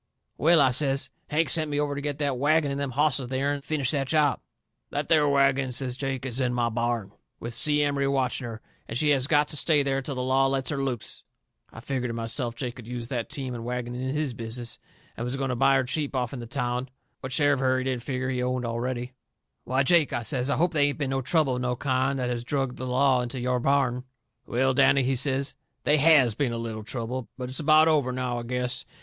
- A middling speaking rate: No, fast, 250 wpm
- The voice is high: No, low, 130 Hz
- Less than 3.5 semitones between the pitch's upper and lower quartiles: Yes, narrow, 2.4 semitones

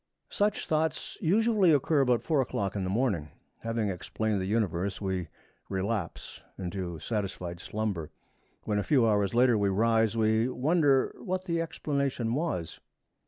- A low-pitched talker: Yes, low, 110 Hz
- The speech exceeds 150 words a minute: No, average, 145 wpm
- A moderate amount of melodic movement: No, wide, 6.2 semitones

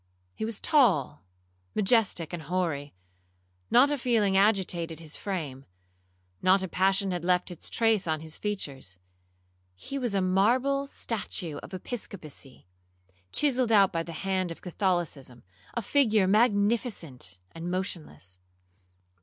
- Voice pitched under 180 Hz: No, medium, 185 Hz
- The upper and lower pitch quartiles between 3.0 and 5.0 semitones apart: No, wide, 5.4 semitones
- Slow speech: Yes, slow, 120 wpm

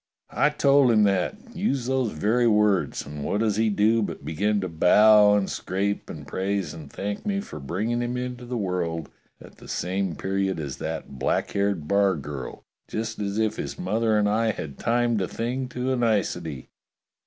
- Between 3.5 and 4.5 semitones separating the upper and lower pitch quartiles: Yes, average, 4.2 semitones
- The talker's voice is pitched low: Yes, low, 105 Hz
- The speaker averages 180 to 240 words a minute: Yes, average, 185 wpm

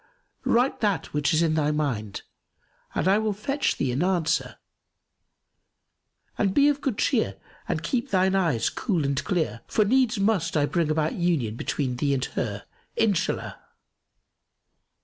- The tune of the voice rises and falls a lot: Yes, wide, 6.4 semitones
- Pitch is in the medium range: Yes, medium, 170 Hz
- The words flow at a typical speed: Yes, average, 150 wpm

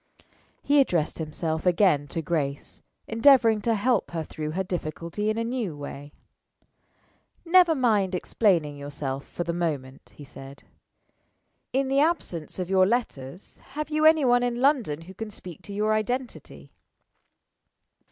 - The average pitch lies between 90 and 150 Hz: No, high, 190 Hz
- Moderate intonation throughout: No, wide, 7.9 semitones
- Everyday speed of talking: Yes, average, 145 wpm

